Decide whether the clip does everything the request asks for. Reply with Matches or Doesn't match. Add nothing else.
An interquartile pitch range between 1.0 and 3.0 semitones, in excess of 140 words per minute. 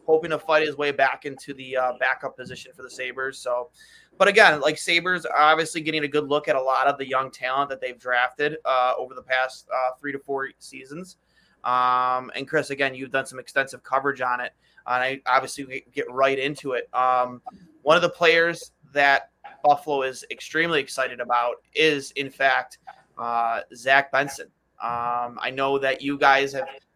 Matches